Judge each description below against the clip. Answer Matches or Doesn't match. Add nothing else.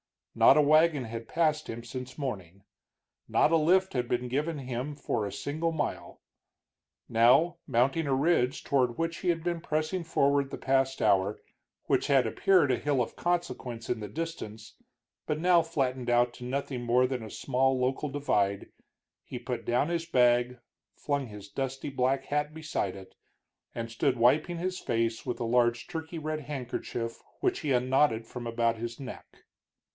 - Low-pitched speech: Matches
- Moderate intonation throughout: Matches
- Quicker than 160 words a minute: Matches